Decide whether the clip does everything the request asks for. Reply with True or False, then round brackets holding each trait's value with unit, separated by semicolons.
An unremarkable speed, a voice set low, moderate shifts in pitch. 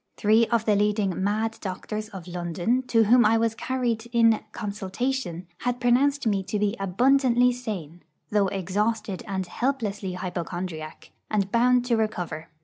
False (145 wpm; 215 Hz; 4.0 semitones)